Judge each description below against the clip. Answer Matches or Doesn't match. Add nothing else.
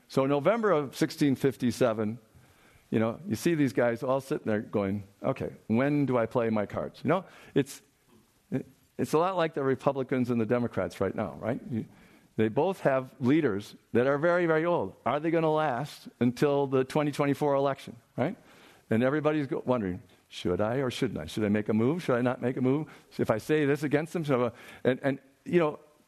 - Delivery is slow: Doesn't match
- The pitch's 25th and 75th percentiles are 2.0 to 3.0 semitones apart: Doesn't match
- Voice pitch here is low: Matches